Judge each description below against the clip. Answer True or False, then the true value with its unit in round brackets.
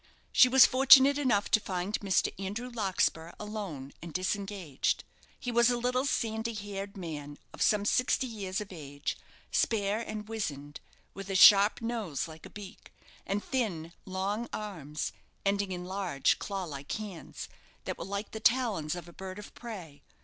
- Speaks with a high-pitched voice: True (200 Hz)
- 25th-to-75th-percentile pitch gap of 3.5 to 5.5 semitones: True (4.0 semitones)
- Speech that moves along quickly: False (165 wpm)